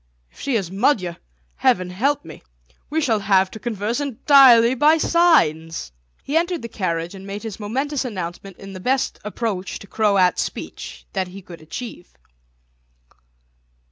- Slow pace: No, average, 150 wpm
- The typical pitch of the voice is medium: No, high, 210 Hz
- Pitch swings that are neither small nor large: No, wide, 6.1 semitones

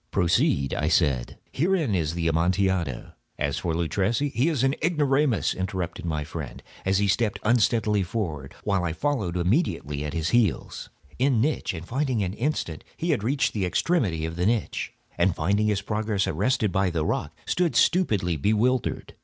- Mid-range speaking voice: No, low, 100 Hz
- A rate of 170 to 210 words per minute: No, average, 160 wpm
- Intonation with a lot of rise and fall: Yes, wide, 6.5 semitones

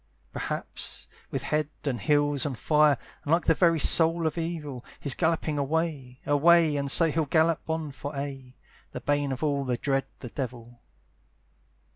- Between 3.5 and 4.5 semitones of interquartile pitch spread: No, average, 2.9 semitones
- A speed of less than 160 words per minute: No, average, 165 wpm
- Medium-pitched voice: Yes, medium, 145 Hz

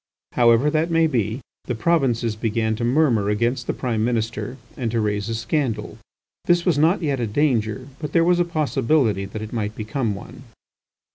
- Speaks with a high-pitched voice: No, low, 120 Hz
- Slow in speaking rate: No, average, 185 wpm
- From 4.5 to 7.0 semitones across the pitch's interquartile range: Yes, average, 5.3 semitones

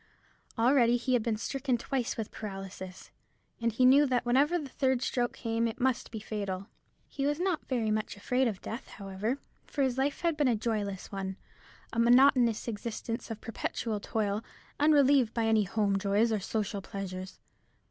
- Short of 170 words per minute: No, average, 175 wpm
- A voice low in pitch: No, high, 230 Hz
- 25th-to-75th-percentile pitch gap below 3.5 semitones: No, average, 3.9 semitones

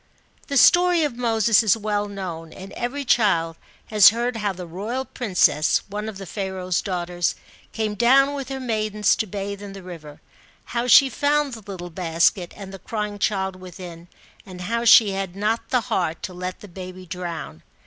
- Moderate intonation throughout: Yes, average, 4.1 semitones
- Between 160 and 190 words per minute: Yes, average, 180 wpm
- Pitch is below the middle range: No, high, 200 Hz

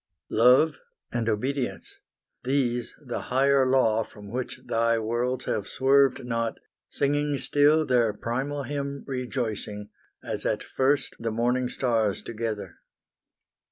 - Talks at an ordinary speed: No, slow, 120 wpm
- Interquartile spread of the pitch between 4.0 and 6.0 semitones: No, average, 3.1 semitones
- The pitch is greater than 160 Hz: No, low, 125 Hz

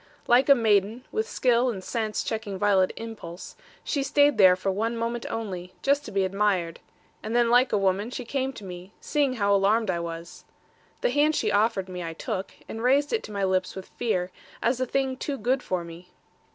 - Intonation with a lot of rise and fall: No, average, 4.9 semitones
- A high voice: Yes, high, 215 Hz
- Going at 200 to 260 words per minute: Yes, fast, 205 wpm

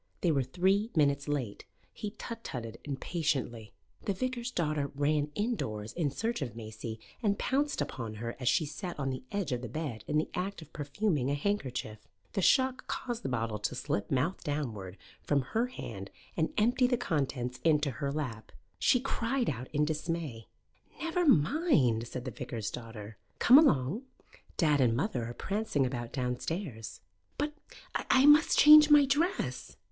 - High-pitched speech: No, medium, 150 Hz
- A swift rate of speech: No, average, 165 wpm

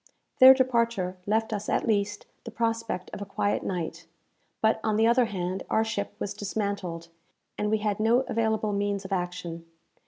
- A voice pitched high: Yes, high, 210 Hz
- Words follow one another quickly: No, average, 175 wpm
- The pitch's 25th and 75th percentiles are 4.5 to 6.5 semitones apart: No, average, 2.8 semitones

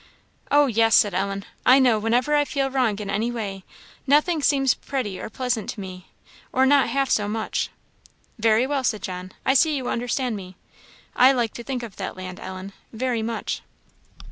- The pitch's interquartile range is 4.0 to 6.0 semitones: Yes, average, 4.6 semitones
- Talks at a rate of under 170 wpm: No, average, 185 wpm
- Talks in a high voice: Yes, high, 235 Hz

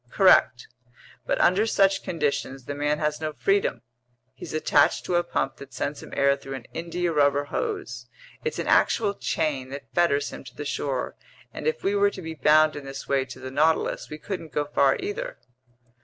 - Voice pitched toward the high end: No, medium, 150 Hz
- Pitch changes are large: No, average, 4.6 semitones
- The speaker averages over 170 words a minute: Yes, average, 195 wpm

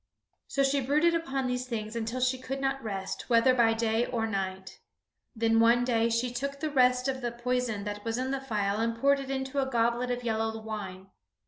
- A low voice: No, high, 240 Hz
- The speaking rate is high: Yes, fast, 210 wpm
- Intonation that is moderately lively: Yes, average, 3.0 semitones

